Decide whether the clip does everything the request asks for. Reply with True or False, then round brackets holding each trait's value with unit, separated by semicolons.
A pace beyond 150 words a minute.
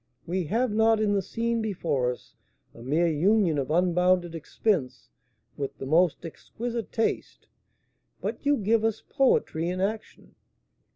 False (140 wpm)